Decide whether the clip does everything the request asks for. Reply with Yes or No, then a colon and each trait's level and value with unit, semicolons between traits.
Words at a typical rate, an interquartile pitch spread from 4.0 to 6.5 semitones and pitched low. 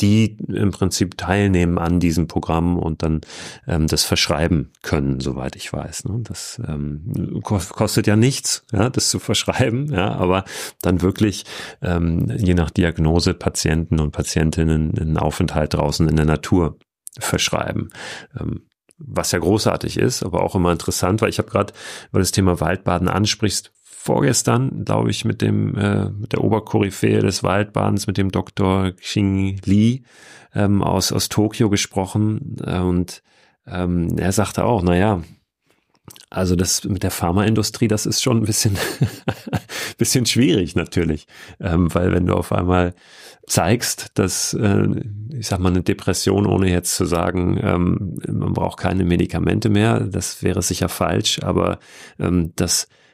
No: average, 150 wpm; average, 3.5 semitones; very low, 95 Hz